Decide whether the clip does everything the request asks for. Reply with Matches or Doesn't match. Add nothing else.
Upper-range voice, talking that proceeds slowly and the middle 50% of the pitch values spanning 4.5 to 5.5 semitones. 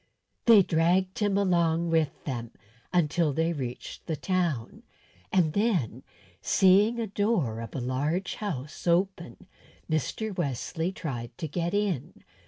Doesn't match